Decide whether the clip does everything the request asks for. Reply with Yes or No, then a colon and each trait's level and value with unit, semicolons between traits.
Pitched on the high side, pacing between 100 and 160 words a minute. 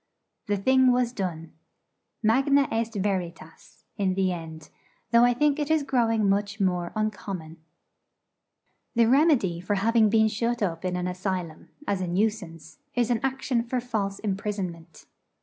Yes: high, 205 Hz; average, 150 wpm